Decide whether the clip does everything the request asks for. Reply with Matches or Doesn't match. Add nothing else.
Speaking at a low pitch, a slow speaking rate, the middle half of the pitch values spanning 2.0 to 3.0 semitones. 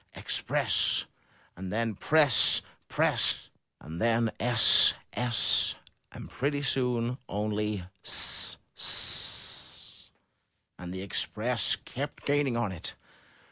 Doesn't match